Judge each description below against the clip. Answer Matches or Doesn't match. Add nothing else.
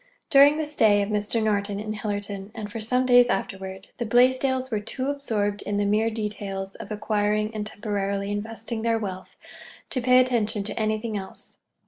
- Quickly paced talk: Doesn't match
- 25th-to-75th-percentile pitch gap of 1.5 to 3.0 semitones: Matches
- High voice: Matches